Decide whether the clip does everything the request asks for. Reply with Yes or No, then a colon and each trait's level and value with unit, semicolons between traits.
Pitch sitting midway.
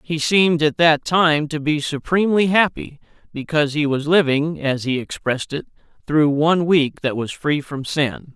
Yes: medium, 150 Hz